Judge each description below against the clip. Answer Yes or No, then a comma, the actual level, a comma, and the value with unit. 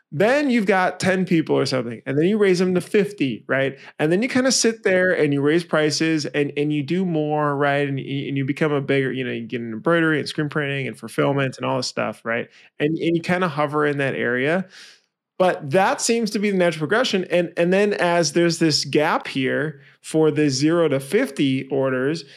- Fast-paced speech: Yes, fast, 230 wpm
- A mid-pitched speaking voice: Yes, medium, 155 Hz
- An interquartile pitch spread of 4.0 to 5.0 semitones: Yes, average, 4.5 semitones